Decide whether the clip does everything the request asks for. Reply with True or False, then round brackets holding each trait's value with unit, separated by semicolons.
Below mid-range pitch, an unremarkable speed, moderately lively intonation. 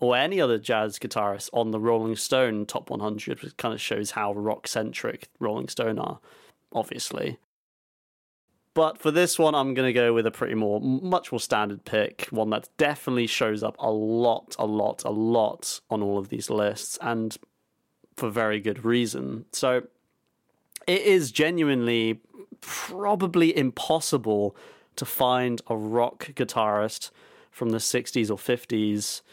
True (115 Hz; 150 wpm; 3.5 semitones)